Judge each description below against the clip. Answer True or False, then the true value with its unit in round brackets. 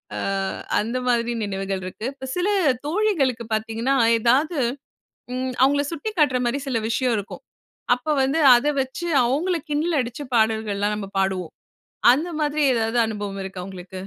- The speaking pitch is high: True (245 Hz)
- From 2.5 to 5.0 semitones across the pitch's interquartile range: False (5.4 semitones)